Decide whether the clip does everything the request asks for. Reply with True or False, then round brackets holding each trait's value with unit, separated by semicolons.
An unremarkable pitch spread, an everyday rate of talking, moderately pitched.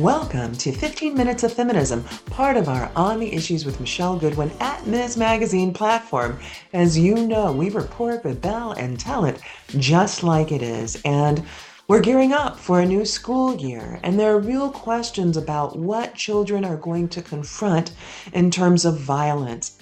False (7.2 semitones; 175 wpm; 180 Hz)